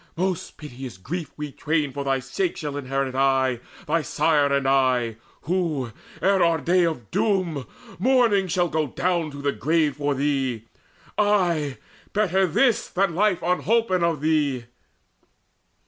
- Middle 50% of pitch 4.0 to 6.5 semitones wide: Yes, average, 4.9 semitones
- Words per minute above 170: No, average, 145 wpm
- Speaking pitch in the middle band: Yes, medium, 155 Hz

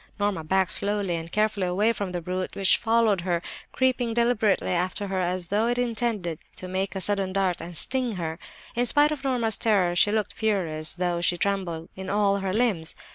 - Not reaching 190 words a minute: No, average, 195 wpm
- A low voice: No, high, 195 Hz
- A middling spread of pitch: Yes, average, 3.7 semitones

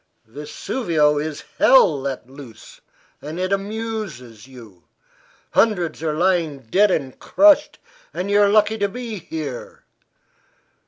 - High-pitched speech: No, medium, 165 Hz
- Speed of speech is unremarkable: No, slow, 120 wpm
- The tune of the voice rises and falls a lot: Yes, wide, 7.0 semitones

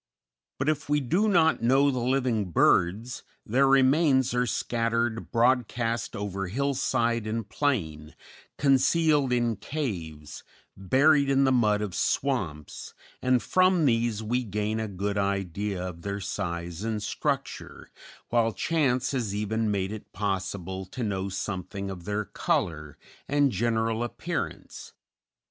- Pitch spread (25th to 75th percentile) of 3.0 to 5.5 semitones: Yes, average, 5.0 semitones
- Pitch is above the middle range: No, low, 115 Hz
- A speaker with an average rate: No, slow, 130 wpm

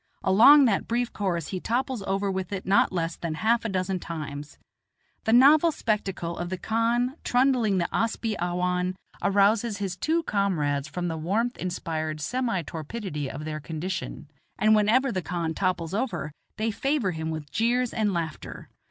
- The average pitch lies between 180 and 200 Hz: Yes, high, 190 Hz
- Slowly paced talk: No, average, 170 wpm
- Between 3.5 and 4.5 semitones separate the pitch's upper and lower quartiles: No, average, 5.3 semitones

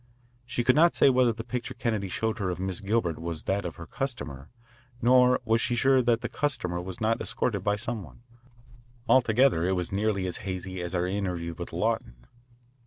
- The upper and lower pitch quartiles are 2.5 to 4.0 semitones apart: No, average, 5.1 semitones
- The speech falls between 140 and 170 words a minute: No, average, 195 wpm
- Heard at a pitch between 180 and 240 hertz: No, low, 105 Hz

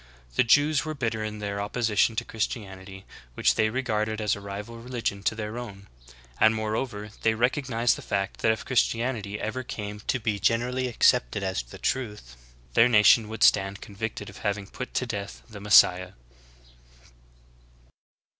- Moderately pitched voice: No, low, 110 Hz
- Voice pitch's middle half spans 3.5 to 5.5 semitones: No, average, 2.7 semitones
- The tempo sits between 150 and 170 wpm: Yes, average, 165 wpm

